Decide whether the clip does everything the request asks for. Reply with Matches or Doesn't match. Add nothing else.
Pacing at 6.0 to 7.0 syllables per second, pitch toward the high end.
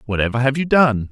Doesn't match